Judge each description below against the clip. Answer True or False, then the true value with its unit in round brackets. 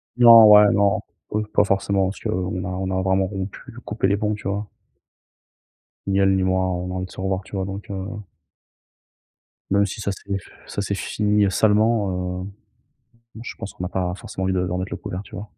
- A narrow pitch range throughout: True (1.7 semitones)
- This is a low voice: True (95 Hz)